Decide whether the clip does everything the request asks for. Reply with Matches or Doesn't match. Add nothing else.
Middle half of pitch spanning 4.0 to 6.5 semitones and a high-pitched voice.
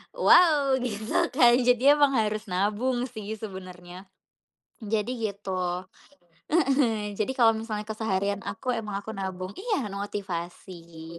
Matches